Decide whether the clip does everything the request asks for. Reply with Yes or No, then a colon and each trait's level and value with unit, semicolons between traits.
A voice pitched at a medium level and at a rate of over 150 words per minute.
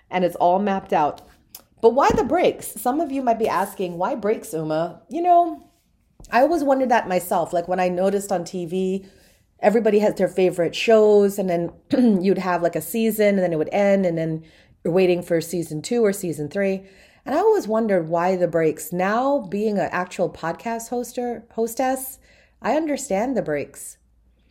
No: high, 195 Hz; average, 185 wpm